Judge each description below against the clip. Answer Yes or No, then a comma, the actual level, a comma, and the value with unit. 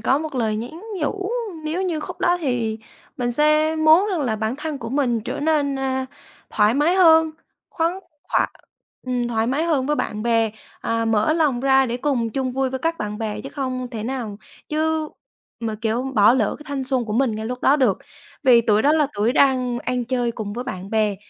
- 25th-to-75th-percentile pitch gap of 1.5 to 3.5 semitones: No, average, 4.8 semitones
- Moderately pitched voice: No, very high, 255 Hz